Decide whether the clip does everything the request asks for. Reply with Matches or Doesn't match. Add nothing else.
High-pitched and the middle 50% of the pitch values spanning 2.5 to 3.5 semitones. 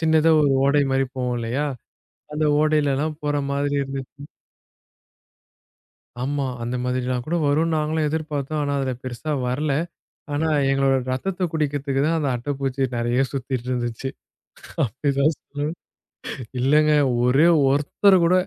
Doesn't match